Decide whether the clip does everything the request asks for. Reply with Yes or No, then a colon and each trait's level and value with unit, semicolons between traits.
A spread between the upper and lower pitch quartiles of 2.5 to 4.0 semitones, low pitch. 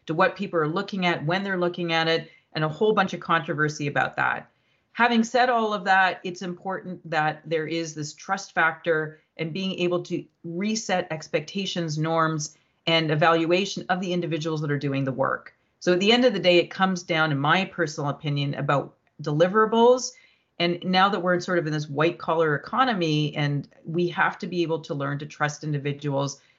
No: average, 3.2 semitones; medium, 170 Hz